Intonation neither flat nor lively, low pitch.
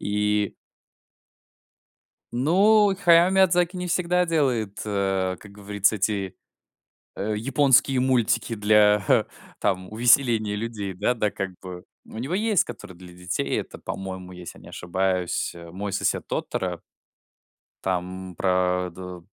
No: wide, 5.8 semitones; low, 105 Hz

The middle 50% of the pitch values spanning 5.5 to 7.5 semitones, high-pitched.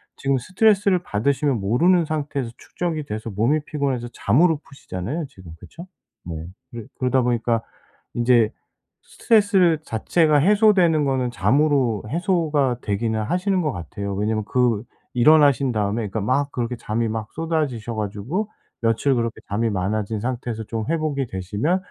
No: wide, 6.0 semitones; low, 125 Hz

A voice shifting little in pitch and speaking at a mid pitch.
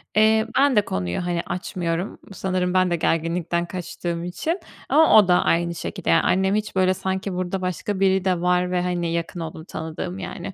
Yes: narrow, 1.9 semitones; medium, 180 Hz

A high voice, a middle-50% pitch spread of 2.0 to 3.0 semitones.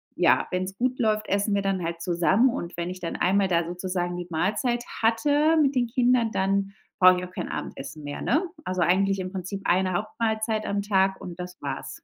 No: high, 195 Hz; average, 3.6 semitones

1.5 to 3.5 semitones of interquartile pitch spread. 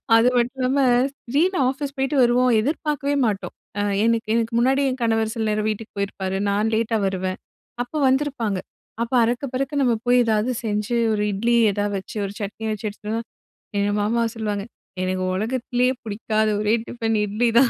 Yes: average, 3.2 semitones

